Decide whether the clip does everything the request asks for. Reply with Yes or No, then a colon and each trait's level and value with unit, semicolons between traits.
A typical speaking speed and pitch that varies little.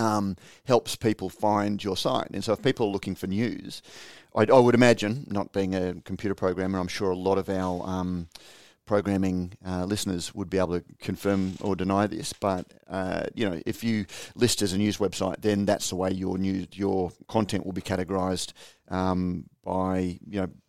Yes: average, 195 wpm; narrow, 1.9 semitones